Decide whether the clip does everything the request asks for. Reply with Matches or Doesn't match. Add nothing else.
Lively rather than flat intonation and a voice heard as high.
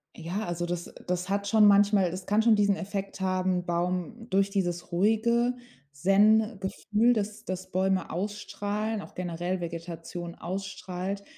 Doesn't match